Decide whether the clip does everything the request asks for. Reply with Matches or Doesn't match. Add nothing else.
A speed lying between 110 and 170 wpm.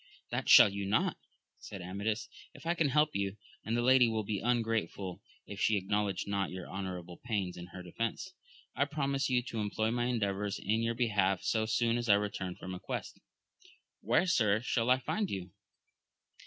Doesn't match